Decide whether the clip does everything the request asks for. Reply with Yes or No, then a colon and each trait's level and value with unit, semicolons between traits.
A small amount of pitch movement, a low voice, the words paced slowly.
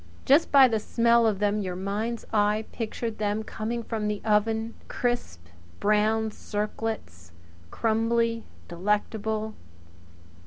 No: narrow, 1.6 semitones; high, 220 Hz; slow, 120 wpm